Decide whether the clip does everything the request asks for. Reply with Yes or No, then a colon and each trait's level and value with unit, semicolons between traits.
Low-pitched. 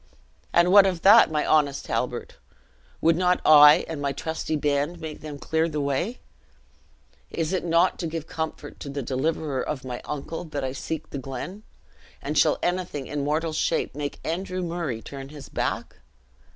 No: medium, 155 Hz